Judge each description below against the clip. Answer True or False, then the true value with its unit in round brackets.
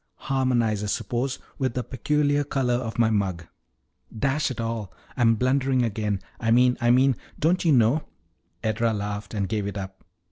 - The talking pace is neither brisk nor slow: True (175 wpm)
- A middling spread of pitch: True (3.7 semitones)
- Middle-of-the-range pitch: False (120 Hz)